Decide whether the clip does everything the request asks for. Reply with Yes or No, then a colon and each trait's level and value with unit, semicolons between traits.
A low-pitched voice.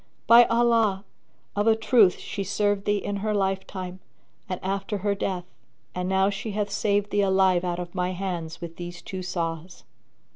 No: high, 195 Hz